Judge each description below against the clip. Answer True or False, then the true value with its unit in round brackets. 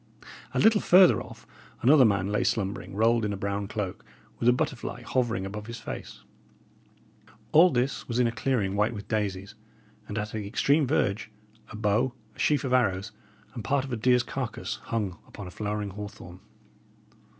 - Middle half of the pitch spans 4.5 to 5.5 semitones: False (3.6 semitones)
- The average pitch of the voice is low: True (110 Hz)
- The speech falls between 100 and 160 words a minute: False (175 wpm)